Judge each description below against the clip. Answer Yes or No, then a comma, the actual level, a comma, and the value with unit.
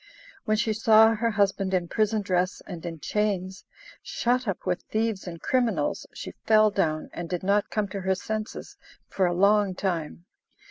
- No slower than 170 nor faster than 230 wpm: Yes, average, 175 wpm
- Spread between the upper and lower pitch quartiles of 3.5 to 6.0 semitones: No, average, 2.9 semitones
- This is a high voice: Yes, high, 200 Hz